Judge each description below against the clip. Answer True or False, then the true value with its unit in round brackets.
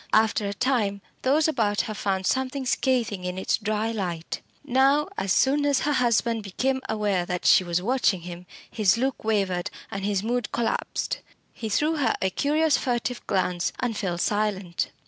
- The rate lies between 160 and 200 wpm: True (170 wpm)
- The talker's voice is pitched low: False (215 Hz)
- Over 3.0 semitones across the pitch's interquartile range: True (5.2 semitones)